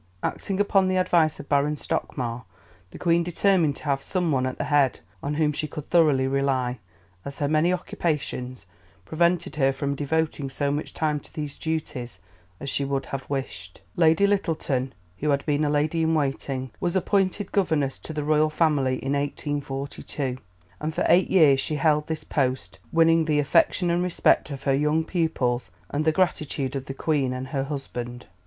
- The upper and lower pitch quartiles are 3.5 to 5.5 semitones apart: No, average, 2.9 semitones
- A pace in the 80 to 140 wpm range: No, average, 180 wpm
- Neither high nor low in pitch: Yes, medium, 150 Hz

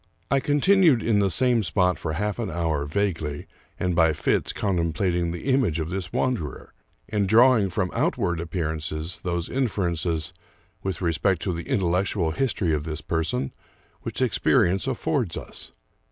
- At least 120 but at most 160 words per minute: Yes, average, 155 wpm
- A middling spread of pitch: Yes, average, 4.6 semitones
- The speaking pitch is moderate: No, very low, 90 Hz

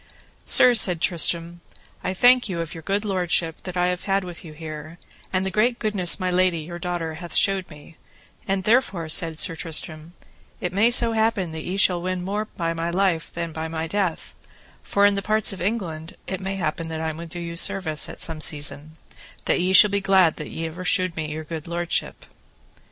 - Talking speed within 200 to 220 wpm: Yes, fast, 205 wpm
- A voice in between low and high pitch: Yes, medium, 175 Hz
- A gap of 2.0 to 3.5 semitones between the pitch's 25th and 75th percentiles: Yes, average, 3.1 semitones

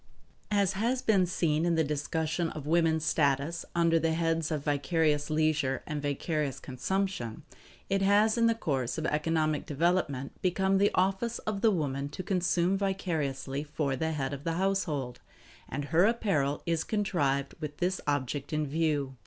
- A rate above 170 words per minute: No, average, 160 wpm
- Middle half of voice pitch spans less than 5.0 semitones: Yes, average, 4.4 semitones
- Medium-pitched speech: Yes, medium, 160 Hz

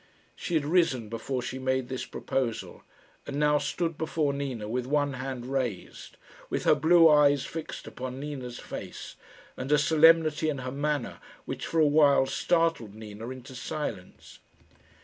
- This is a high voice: No, medium, 140 Hz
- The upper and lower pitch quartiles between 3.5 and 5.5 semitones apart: No, average, 3.1 semitones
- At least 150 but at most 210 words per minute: Yes, average, 155 wpm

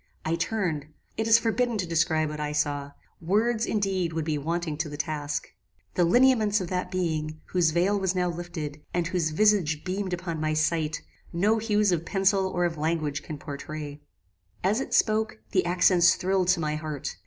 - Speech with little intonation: No, average, 3.9 semitones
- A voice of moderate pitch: Yes, medium, 170 Hz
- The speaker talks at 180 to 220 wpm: Yes, average, 185 wpm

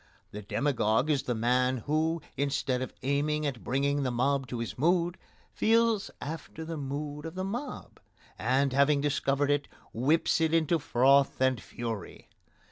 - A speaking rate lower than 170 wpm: Yes, average, 155 wpm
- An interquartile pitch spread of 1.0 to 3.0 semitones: No, average, 3.5 semitones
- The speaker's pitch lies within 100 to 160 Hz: Yes, medium, 140 Hz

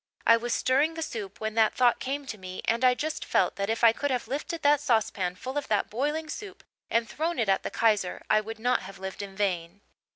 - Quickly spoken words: Yes, fast, 240 wpm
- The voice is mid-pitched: No, high, 230 Hz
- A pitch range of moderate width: No, wide, 5.8 semitones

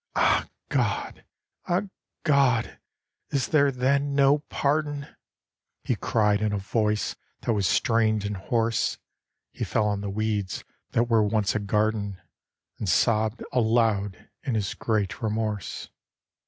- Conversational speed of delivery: No, slow, 130 wpm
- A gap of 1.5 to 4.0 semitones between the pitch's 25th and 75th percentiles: Yes, average, 3.3 semitones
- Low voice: Yes, low, 110 Hz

